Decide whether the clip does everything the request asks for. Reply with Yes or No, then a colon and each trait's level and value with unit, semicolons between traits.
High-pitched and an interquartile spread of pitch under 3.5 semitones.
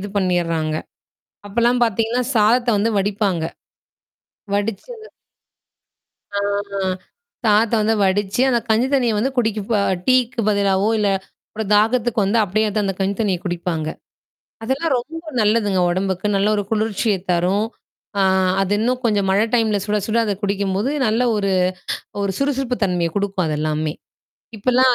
Yes: high, 210 Hz; average, 3.1 semitones